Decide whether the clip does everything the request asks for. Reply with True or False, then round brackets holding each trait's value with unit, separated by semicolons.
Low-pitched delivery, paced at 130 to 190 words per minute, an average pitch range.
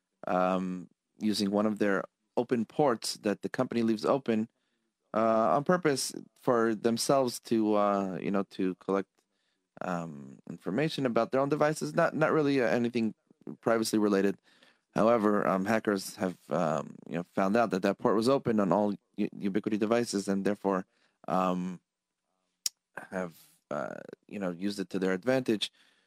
True (105 Hz; 150 wpm; 3.6 semitones)